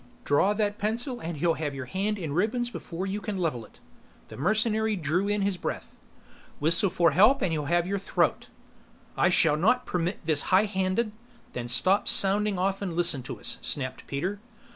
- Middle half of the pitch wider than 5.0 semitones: No, average, 4.3 semitones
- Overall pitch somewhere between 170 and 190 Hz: Yes, medium, 185 Hz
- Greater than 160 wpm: Yes, average, 190 wpm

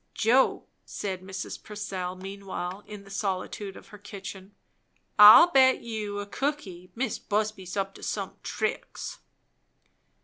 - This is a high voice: Yes, high, 200 Hz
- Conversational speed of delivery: No, slow, 130 wpm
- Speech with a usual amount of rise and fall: No, narrow, 2.0 semitones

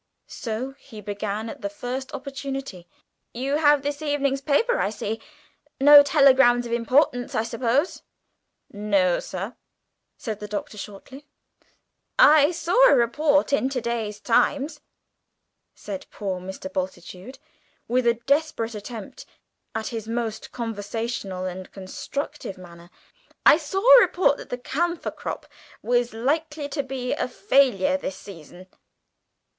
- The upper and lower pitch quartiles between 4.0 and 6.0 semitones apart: Yes, average, 5.3 semitones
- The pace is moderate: No, slow, 130 wpm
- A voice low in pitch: No, high, 245 Hz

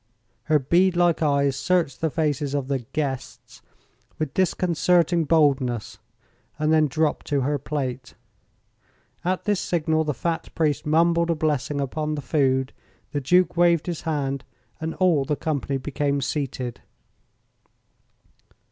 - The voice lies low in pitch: No, medium, 150 Hz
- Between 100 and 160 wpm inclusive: Yes, slow, 135 wpm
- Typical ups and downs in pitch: Yes, average, 3.2 semitones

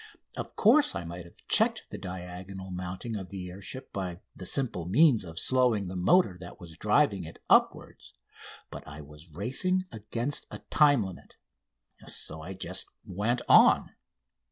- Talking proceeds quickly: No, average, 165 wpm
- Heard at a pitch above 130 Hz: No, very low, 95 Hz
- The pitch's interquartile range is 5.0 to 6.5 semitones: Yes, average, 5.3 semitones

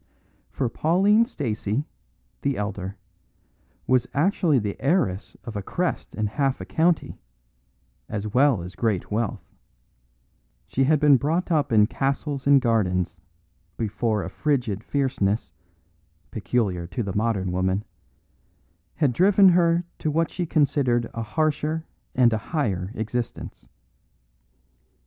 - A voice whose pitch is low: Yes, low, 125 Hz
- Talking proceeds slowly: Yes, slow, 125 wpm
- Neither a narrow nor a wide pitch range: No, wide, 6.4 semitones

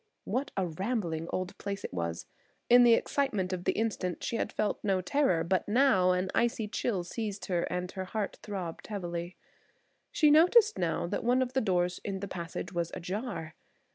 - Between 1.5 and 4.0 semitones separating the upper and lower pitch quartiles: No, average, 4.4 semitones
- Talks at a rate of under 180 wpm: No, average, 185 wpm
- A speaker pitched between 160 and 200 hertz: Yes, high, 190 Hz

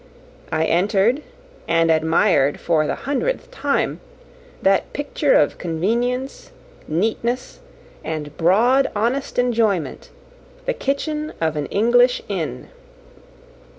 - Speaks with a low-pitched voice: No, high, 210 Hz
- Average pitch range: No, wide, 7.5 semitones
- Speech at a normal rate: No, slow, 100 wpm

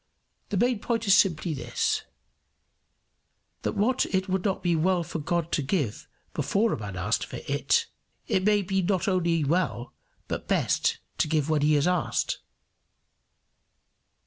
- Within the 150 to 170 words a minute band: Yes, average, 160 wpm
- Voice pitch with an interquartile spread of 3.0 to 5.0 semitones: Yes, average, 4.0 semitones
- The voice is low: No, medium, 175 Hz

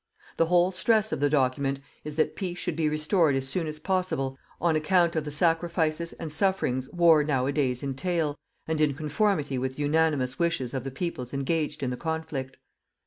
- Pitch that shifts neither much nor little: Yes, average, 3.8 semitones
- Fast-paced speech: No, average, 185 wpm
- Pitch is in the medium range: Yes, medium, 155 Hz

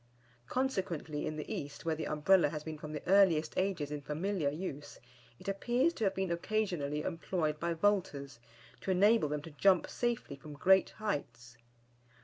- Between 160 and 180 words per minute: Yes, average, 165 wpm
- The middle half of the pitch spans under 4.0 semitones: No, average, 4.5 semitones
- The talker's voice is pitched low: No, medium, 165 Hz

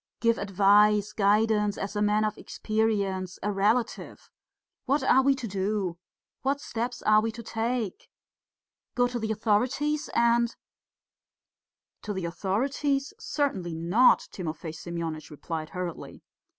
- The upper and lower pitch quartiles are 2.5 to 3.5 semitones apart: No, average, 3.9 semitones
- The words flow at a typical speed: No, slow, 130 wpm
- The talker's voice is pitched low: No, high, 210 Hz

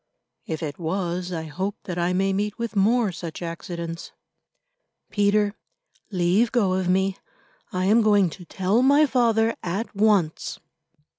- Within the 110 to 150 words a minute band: Yes, average, 145 wpm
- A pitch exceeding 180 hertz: Yes, high, 190 Hz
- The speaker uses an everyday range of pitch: Yes, average, 3.4 semitones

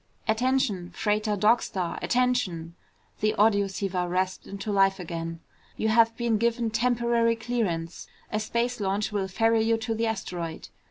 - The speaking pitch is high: Yes, high, 215 Hz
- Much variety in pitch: No, average, 3.4 semitones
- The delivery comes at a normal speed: Yes, average, 145 wpm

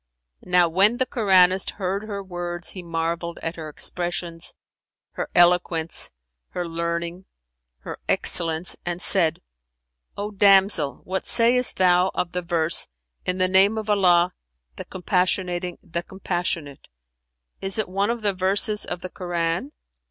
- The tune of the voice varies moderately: No, narrow, 2.2 semitones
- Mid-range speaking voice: Yes, medium, 180 Hz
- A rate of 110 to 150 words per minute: Yes, average, 140 wpm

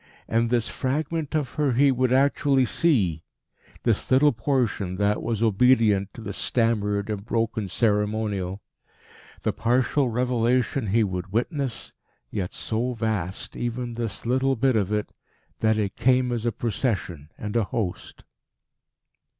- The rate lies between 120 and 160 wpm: Yes, average, 140 wpm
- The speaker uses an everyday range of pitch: Yes, average, 3.7 semitones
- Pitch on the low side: Yes, low, 115 Hz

